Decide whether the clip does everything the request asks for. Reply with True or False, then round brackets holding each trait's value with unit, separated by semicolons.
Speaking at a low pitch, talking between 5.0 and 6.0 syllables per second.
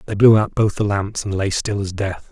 True (100 Hz; 5.2 syllables/s)